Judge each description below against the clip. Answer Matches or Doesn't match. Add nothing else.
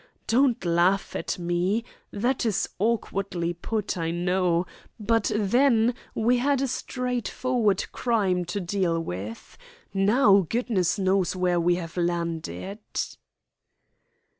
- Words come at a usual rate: Doesn't match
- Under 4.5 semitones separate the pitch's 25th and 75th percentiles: Doesn't match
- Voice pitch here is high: Matches